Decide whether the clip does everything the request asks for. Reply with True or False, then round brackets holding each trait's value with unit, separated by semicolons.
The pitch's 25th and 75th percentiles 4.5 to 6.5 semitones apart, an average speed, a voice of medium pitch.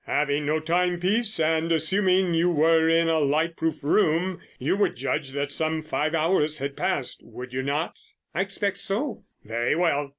False (3.2 semitones; 175 wpm; 160 Hz)